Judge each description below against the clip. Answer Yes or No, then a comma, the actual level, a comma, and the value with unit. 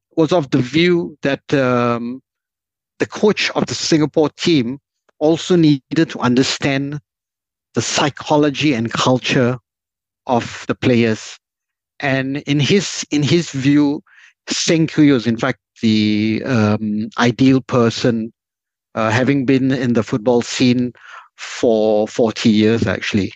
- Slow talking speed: Yes, slow, 125 wpm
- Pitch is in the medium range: No, low, 130 Hz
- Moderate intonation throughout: Yes, average, 4.3 semitones